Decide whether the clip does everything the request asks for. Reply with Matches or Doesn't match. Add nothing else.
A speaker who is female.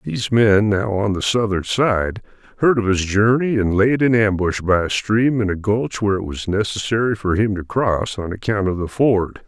Doesn't match